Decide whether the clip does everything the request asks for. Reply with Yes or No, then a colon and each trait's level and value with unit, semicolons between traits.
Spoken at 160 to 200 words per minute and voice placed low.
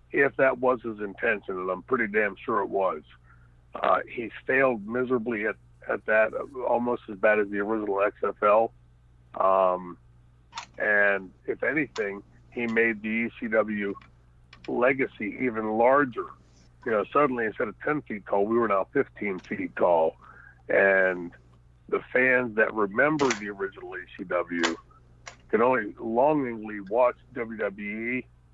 No: slow, 135 wpm; low, 100 Hz